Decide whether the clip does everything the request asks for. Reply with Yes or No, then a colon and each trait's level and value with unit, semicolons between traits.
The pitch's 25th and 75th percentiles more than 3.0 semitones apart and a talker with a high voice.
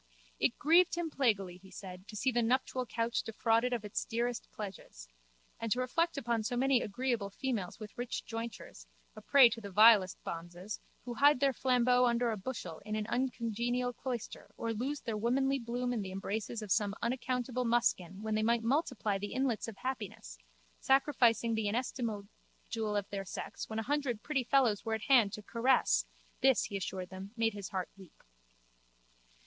Yes: average, 3.4 semitones; high, 230 Hz